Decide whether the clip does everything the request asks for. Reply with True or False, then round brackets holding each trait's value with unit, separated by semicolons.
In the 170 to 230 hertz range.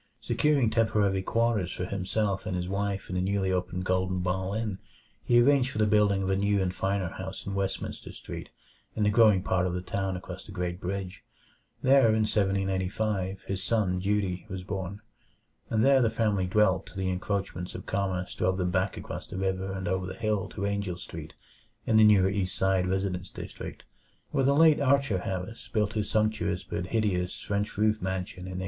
False (95 Hz)